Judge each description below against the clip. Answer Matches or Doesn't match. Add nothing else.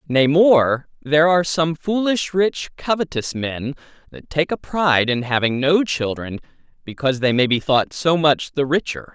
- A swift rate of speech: Doesn't match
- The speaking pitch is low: Doesn't match